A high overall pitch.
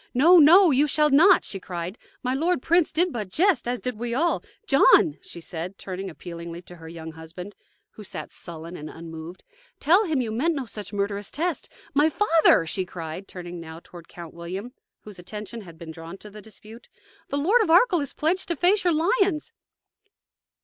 Yes: high, 215 Hz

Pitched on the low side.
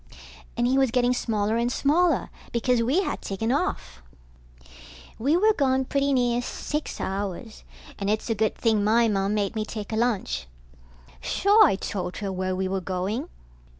No: high, 225 Hz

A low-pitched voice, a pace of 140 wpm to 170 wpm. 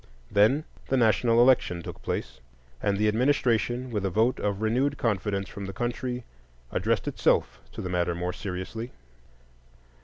Yes: low, 110 Hz; average, 150 wpm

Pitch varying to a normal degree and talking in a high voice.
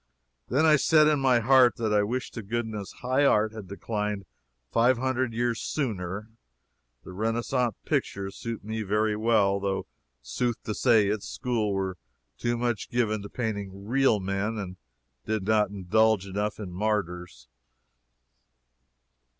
No: average, 3.2 semitones; low, 110 Hz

